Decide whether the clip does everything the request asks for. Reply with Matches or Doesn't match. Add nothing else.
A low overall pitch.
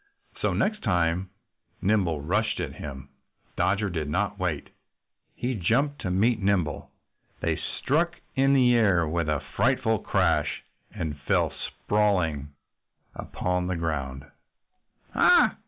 Matches